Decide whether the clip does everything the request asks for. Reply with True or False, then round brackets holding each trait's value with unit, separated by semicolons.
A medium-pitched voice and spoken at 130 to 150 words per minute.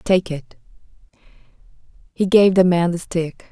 True (175 Hz; 135 wpm)